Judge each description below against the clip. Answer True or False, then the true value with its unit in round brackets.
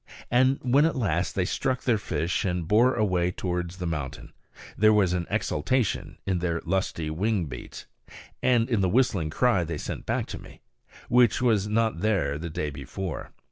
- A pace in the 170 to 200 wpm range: True (180 wpm)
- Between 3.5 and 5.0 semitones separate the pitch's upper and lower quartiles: False (5.4 semitones)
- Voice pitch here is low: True (95 Hz)